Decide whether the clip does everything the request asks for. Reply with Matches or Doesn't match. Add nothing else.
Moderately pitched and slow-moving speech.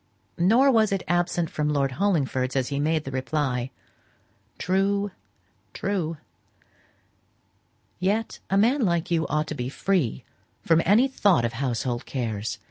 Matches